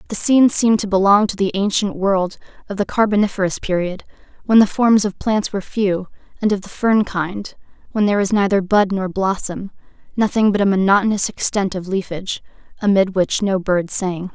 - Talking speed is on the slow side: No, average, 185 wpm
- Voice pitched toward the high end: Yes, high, 200 Hz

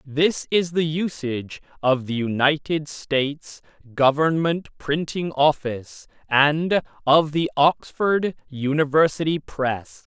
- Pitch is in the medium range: Yes, medium, 150 Hz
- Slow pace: Yes, slow, 100 wpm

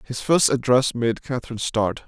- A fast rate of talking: No, average, 175 wpm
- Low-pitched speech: Yes, low, 120 Hz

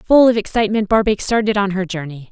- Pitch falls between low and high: No, high, 205 Hz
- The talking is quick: Yes, fast, 210 wpm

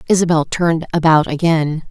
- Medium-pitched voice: Yes, medium, 160 Hz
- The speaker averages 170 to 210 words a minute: No, slow, 125 wpm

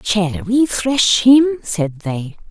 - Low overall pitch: No, high, 215 Hz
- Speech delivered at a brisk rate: No, average, 145 wpm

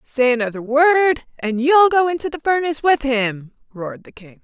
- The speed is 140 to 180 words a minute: No, average, 190 wpm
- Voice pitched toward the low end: No, very high, 275 Hz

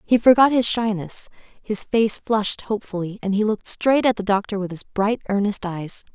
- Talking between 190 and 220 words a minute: Yes, average, 195 wpm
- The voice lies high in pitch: Yes, high, 210 Hz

